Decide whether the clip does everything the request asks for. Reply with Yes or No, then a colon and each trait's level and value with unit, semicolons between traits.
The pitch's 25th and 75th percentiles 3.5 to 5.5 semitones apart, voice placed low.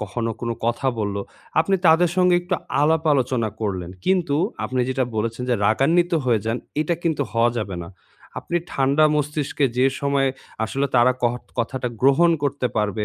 Yes: average, 5.1 semitones; low, 130 Hz